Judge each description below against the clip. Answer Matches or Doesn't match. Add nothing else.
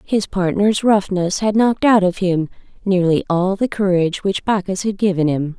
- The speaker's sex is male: Doesn't match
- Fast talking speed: Doesn't match